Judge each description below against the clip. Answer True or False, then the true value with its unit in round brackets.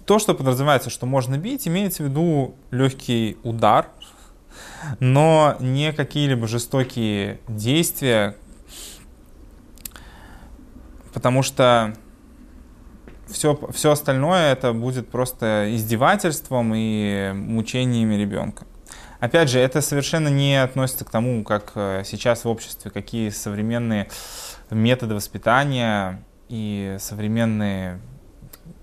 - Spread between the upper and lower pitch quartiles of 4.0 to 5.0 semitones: True (4.4 semitones)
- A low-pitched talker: True (120 Hz)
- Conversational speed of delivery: False (95 wpm)